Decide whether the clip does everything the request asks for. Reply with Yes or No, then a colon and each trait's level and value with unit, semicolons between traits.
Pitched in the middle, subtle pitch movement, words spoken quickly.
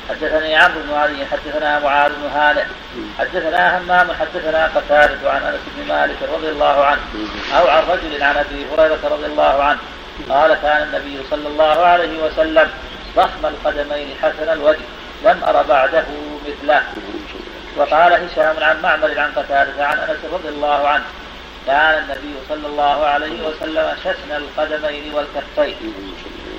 Yes: medium, 150 Hz; narrow, 1.5 semitones; fast, 145 wpm